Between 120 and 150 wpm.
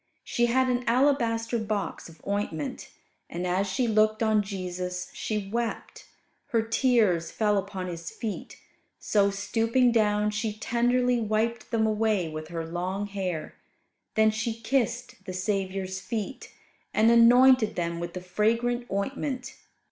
Yes: average, 140 wpm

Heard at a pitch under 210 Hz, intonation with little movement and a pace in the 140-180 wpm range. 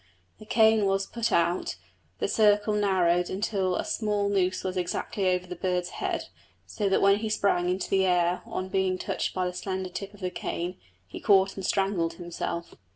No: high, 190 Hz; narrow, 2.0 semitones; average, 190 wpm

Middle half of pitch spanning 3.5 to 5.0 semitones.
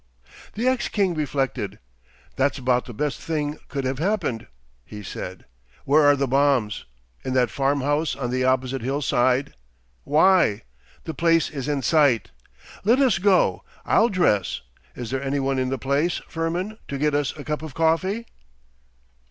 Yes: average, 4.1 semitones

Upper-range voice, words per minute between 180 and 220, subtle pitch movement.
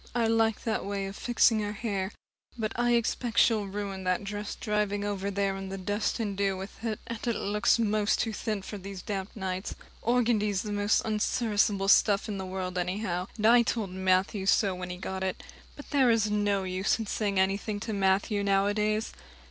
Yes: high, 205 Hz; average, 195 wpm; narrow, 2.1 semitones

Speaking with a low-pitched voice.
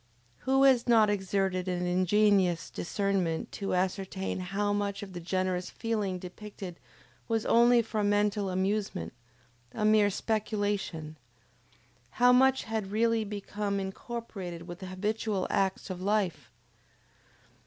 No: high, 200 Hz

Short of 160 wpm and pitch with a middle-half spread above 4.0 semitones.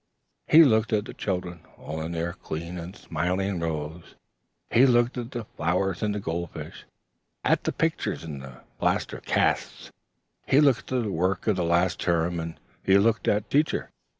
No: average, 180 wpm; average, 4.7 semitones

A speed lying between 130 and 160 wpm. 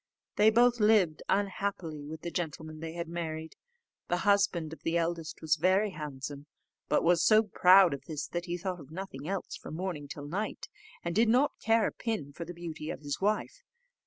No: average, 195 wpm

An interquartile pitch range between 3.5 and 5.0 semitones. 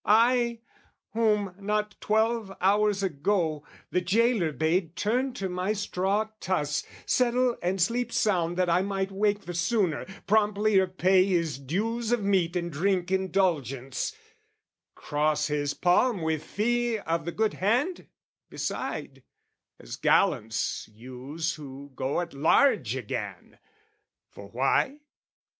Yes: average, 4.7 semitones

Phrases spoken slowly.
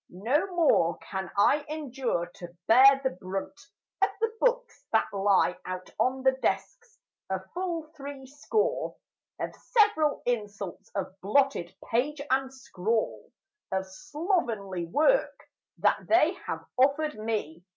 Yes: slow, 130 wpm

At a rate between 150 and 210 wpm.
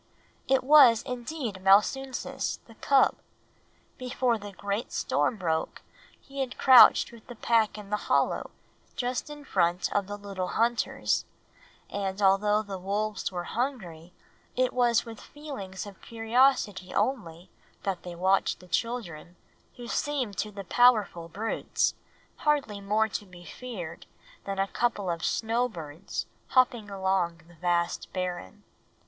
No: slow, 135 wpm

